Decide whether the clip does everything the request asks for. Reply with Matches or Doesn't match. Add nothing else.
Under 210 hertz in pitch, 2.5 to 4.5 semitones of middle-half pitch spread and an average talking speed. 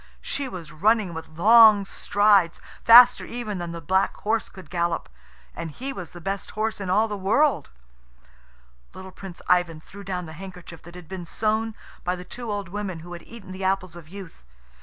Matches